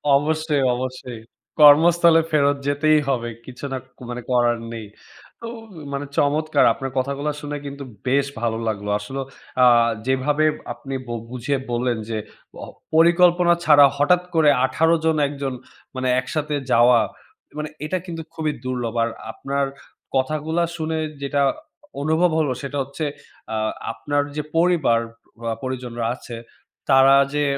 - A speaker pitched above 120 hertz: Yes, medium, 140 Hz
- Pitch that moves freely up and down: No, average, 3.4 semitones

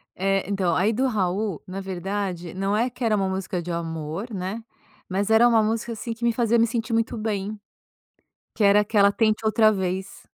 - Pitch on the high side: Yes, high, 205 Hz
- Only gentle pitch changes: No, average, 3.0 semitones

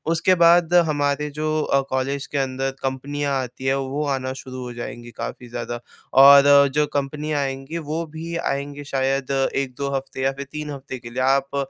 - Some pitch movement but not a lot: No, narrow, 1.7 semitones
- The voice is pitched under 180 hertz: Yes, medium, 140 Hz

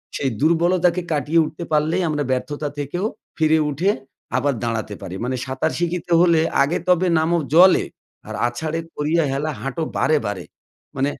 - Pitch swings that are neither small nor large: Yes, average, 3.5 semitones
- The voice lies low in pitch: No, medium, 155 Hz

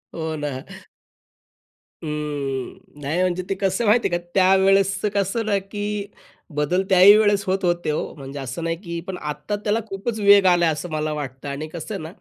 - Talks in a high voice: No, medium, 180 Hz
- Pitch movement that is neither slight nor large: Yes, average, 4.6 semitones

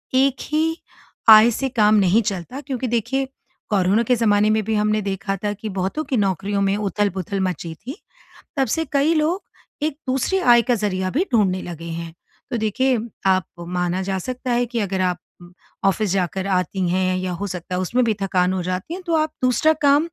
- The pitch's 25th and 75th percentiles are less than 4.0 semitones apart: No, average, 5.3 semitones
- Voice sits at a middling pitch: No, high, 210 Hz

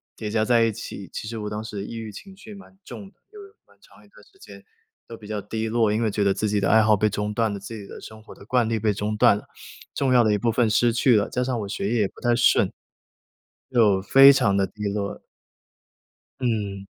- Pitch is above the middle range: No, low, 110 Hz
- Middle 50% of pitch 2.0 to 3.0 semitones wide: Yes, narrow, 2.5 semitones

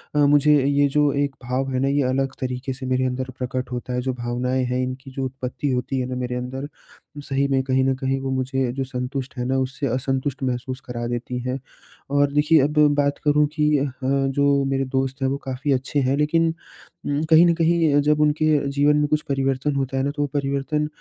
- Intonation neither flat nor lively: No, narrow, 1.8 semitones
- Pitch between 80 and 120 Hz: No, low, 135 Hz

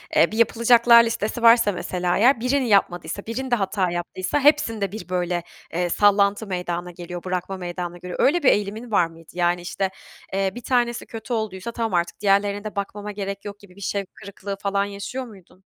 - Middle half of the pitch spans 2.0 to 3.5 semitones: No, average, 3.9 semitones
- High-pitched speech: Yes, high, 200 Hz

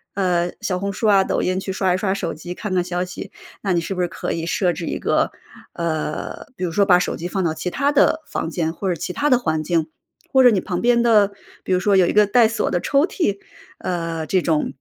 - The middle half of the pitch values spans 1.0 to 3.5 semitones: Yes, average, 3.0 semitones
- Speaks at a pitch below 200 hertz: Yes, medium, 185 Hz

